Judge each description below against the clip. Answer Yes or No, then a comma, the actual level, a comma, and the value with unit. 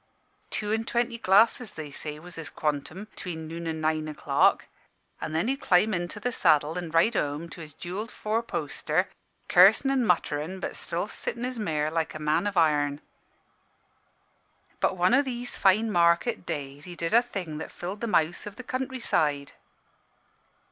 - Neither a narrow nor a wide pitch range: No, wide, 6.1 semitones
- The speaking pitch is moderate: Yes, medium, 175 Hz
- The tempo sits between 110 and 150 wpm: No, average, 170 wpm